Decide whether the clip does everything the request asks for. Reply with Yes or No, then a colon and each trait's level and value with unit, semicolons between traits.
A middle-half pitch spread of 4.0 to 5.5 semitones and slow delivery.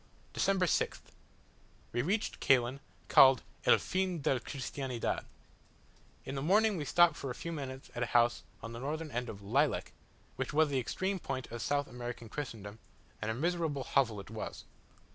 No: average, 4.8 semitones; average, 170 wpm